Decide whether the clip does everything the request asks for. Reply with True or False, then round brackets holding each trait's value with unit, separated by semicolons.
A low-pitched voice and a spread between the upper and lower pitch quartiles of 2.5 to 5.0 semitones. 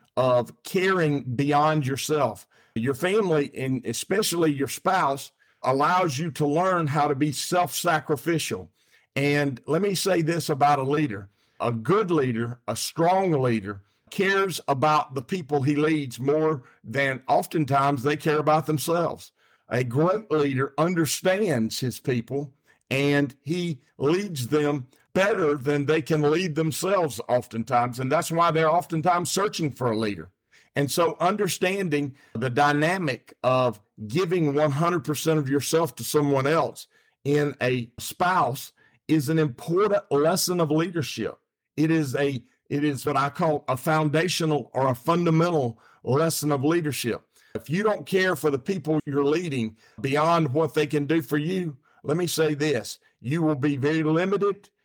False (150 Hz; 3.6 semitones)